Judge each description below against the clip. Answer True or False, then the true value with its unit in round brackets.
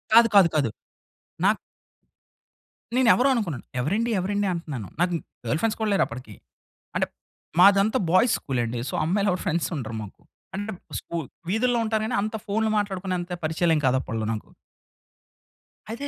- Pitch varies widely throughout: True (6.2 semitones)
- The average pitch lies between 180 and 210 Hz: True (185 Hz)